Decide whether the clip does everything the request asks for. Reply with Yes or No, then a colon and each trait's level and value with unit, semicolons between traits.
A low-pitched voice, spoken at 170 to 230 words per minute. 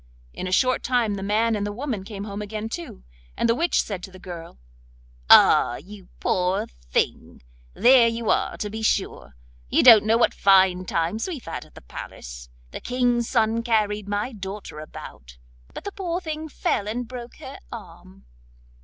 No: high, 210 Hz; average, 185 wpm